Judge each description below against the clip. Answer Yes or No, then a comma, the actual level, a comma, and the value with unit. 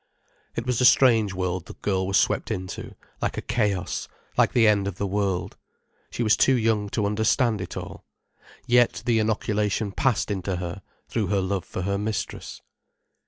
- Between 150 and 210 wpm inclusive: Yes, average, 175 wpm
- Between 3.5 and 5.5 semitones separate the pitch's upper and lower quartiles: No, average, 2.7 semitones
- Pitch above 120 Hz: No, low, 105 Hz